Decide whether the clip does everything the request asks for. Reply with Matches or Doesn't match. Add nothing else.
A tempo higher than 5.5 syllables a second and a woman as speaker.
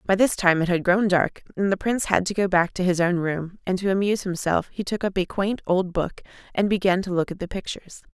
Matches